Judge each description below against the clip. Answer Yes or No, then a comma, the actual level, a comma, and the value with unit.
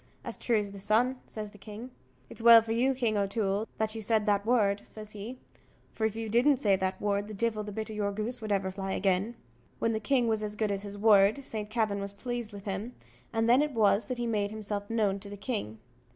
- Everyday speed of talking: No, fast, 245 wpm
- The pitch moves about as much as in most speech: No, narrow, 2.1 semitones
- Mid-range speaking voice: No, high, 215 Hz